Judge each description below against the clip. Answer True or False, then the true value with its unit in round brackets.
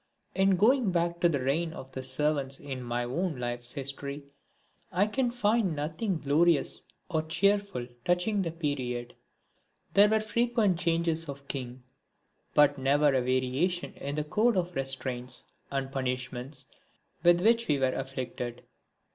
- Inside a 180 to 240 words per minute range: False (145 wpm)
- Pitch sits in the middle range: True (150 Hz)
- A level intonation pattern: False (5.4 semitones)